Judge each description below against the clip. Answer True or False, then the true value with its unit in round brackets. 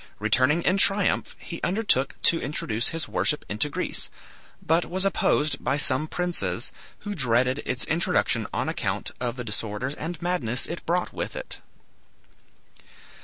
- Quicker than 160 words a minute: False (145 wpm)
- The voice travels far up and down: True (5.9 semitones)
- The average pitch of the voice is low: False (150 Hz)